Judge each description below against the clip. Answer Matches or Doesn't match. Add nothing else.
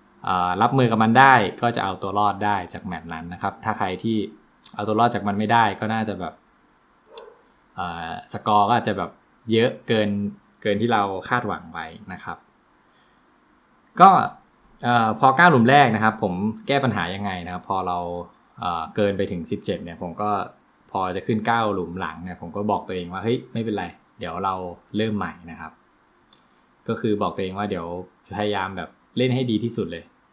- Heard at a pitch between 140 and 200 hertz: Doesn't match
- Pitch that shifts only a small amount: Doesn't match